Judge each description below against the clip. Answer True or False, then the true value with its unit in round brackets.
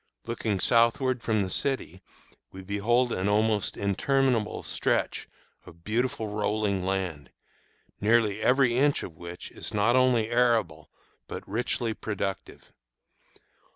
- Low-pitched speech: True (110 Hz)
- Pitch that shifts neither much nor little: True (3.6 semitones)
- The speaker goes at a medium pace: False (120 wpm)